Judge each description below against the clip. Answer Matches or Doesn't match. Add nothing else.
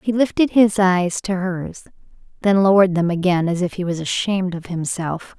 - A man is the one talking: Doesn't match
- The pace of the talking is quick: Doesn't match